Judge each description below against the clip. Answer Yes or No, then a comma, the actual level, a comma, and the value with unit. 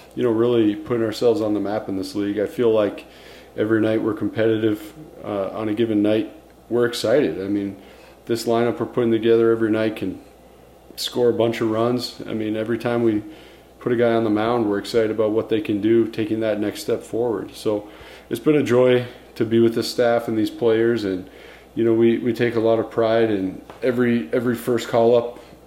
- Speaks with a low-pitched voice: Yes, low, 115 Hz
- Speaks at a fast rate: Yes, fast, 215 wpm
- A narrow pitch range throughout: Yes, narrow, 1.6 semitones